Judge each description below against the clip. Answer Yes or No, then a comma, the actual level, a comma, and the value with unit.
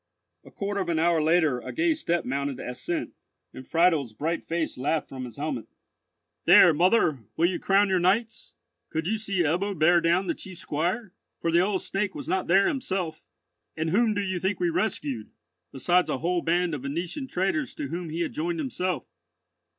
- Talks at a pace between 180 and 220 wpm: Yes, average, 195 wpm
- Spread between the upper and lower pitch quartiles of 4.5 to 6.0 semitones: No, average, 3.6 semitones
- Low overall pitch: No, medium, 175 Hz